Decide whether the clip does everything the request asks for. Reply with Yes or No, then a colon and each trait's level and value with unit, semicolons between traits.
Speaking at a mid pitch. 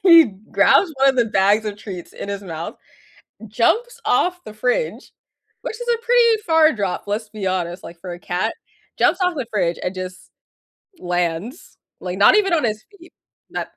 No: high, 215 Hz